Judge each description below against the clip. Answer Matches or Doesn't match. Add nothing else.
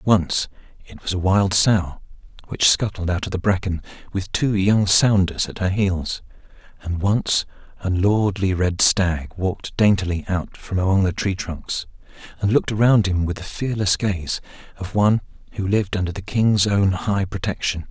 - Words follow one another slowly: Doesn't match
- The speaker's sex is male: Matches